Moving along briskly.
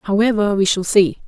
No: average, 190 wpm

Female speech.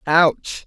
Yes: female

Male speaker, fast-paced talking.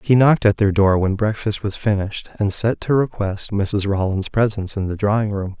Yes: male; fast, 215 wpm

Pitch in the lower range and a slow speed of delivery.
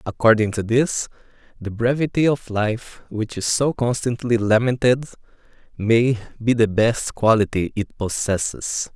Yes: low, 115 Hz; slow, 125 wpm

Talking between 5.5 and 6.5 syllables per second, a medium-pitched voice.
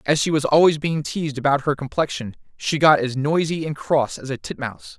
Yes: 5.6 syllables/s; medium, 145 Hz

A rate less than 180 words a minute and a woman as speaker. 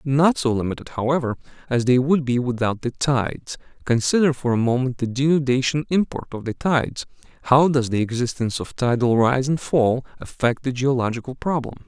No: average, 170 wpm; male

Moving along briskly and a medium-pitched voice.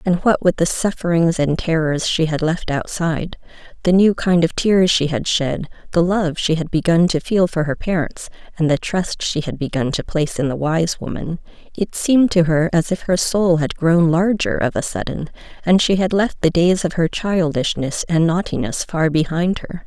Yes: fast, 210 wpm; medium, 170 Hz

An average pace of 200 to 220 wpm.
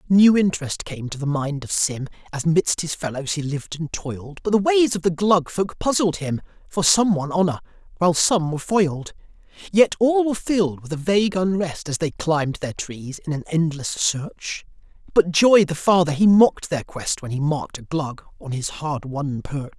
Yes: fast, 205 wpm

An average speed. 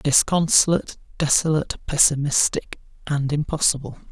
No: slow, 75 wpm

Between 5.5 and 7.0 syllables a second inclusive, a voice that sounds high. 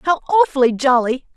Yes: 6.1 syllables/s; very high, 285 Hz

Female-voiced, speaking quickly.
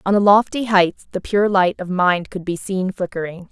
Yes: female; fast, 220 wpm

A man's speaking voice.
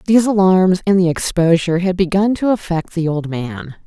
No: female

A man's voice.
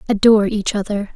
No: female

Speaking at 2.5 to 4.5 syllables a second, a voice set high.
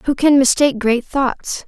Yes: 4.3 syllables/s; very high, 265 Hz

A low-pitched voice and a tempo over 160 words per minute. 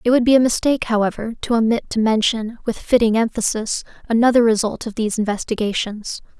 No: high, 225 Hz; average, 170 wpm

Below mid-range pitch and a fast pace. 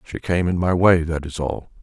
Yes: very low, 85 Hz; fast, 265 wpm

